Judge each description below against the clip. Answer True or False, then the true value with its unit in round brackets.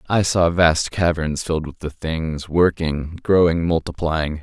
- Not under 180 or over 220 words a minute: False (150 wpm)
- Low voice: True (80 Hz)